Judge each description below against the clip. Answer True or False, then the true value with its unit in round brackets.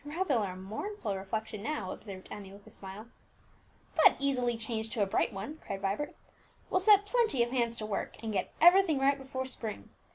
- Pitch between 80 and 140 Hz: False (230 Hz)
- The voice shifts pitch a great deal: True (6.2 semitones)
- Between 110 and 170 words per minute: False (195 wpm)